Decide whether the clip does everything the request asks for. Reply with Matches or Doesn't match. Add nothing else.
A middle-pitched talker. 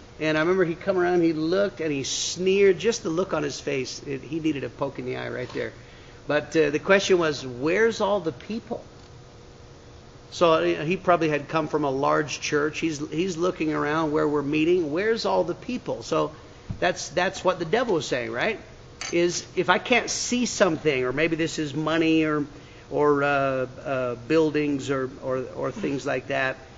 Matches